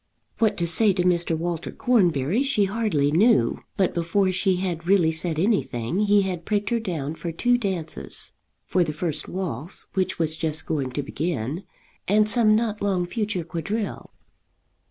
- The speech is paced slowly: No, average, 165 wpm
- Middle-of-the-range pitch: Yes, medium, 180 Hz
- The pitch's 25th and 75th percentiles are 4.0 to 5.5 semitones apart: Yes, average, 4.3 semitones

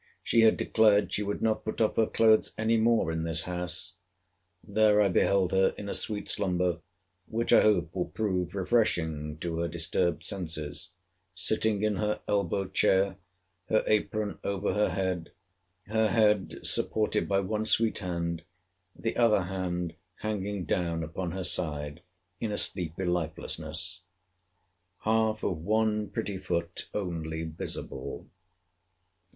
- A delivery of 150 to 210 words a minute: No, average, 140 wpm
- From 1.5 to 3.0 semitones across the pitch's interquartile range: No, average, 3.8 semitones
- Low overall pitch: Yes, very low, 95 Hz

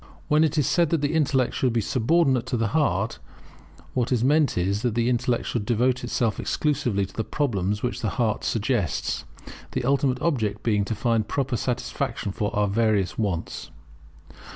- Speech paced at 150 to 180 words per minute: Yes, average, 175 wpm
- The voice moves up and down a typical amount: Yes, average, 4.2 semitones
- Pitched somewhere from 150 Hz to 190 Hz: No, low, 120 Hz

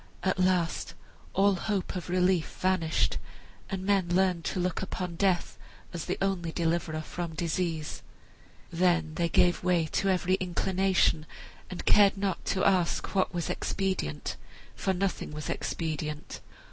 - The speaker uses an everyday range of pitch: No, narrow, 2.2 semitones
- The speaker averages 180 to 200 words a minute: No, average, 140 wpm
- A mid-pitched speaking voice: Yes, medium, 180 Hz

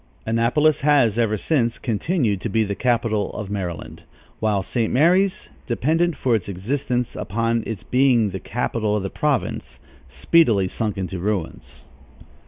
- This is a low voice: Yes, low, 115 Hz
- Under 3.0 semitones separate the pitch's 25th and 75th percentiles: No, average, 4.2 semitones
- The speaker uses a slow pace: No, average, 145 wpm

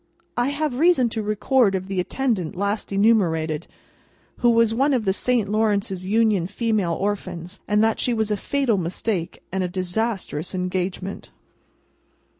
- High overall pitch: Yes, high, 205 Hz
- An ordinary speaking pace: Yes, average, 145 wpm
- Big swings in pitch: No, average, 3.9 semitones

